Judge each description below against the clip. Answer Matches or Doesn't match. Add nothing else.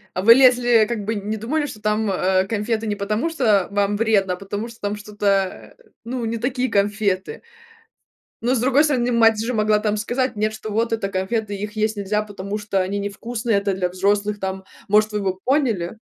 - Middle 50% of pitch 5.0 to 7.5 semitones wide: Doesn't match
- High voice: Matches